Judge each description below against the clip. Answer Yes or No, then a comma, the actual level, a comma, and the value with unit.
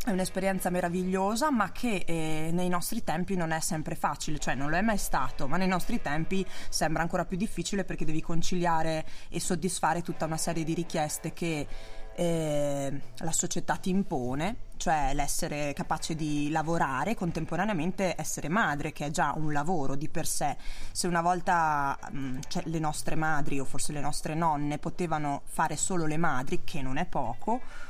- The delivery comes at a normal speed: No, fast, 175 wpm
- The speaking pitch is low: No, medium, 165 Hz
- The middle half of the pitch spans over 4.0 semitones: No, average, 3.2 semitones